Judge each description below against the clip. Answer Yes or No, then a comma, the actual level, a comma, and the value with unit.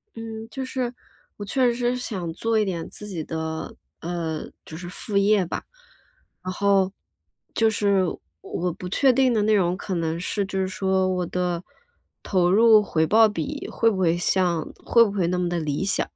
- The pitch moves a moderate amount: Yes, average, 3.8 semitones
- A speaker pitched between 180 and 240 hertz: Yes, high, 190 Hz